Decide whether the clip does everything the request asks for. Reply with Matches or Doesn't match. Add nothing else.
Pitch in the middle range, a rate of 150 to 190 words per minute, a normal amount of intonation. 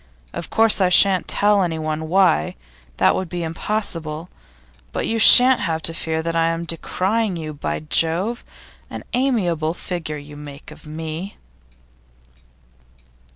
Doesn't match